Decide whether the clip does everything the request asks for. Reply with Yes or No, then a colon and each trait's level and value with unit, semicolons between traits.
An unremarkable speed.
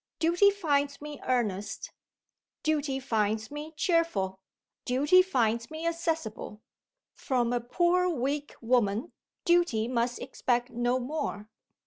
No: slow, 110 wpm